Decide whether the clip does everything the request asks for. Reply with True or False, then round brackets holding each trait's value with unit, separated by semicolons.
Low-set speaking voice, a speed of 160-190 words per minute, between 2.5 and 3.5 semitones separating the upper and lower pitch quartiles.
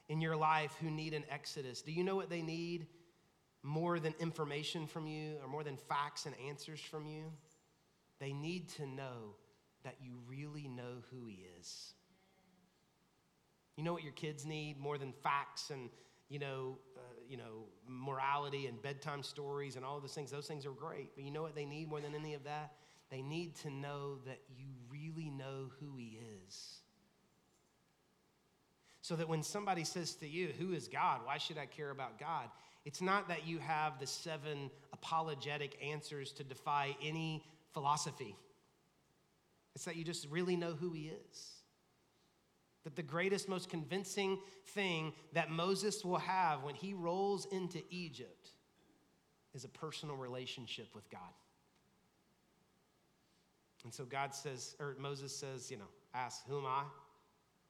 False (150 Hz; 165 wpm; 3.1 semitones)